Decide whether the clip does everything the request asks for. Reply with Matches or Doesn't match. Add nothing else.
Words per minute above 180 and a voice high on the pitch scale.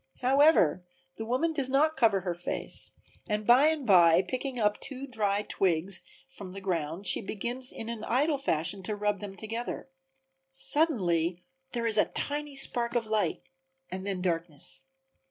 Doesn't match